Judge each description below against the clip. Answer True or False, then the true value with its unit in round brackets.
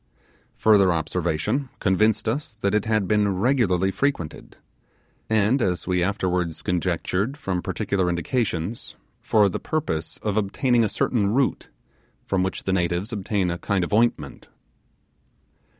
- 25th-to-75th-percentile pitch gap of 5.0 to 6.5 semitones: False (3.6 semitones)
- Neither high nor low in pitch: False (100 Hz)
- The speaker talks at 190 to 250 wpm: False (135 wpm)